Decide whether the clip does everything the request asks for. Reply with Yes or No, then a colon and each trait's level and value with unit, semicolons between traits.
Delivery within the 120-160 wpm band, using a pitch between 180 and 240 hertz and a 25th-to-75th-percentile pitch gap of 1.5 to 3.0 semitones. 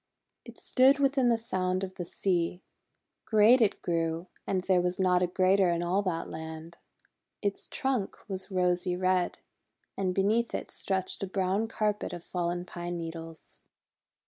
Yes: average, 155 wpm; medium, 185 Hz; narrow, 2.4 semitones